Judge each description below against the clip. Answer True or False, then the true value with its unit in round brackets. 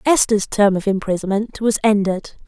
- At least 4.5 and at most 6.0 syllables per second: True (5.0 syllables/s)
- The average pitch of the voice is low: False (205 Hz)